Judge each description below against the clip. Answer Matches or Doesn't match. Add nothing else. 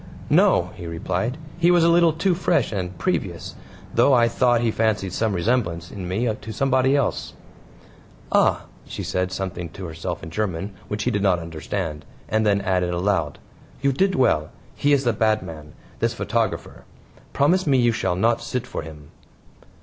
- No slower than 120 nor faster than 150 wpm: Doesn't match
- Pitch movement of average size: Doesn't match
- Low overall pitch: Matches